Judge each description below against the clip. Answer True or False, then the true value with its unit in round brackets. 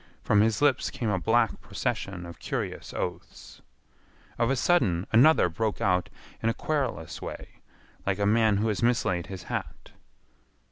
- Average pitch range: True (4.3 semitones)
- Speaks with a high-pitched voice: False (105 Hz)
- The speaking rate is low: False (155 wpm)